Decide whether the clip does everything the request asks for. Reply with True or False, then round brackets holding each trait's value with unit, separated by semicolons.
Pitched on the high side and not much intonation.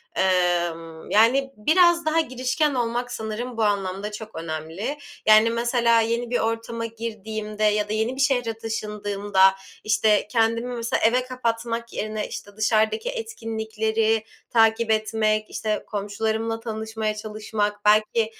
True (220 Hz; 1.7 semitones)